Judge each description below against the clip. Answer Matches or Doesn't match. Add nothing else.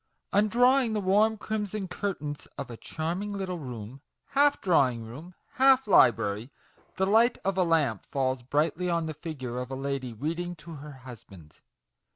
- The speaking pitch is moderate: Matches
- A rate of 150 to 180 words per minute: Matches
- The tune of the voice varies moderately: Doesn't match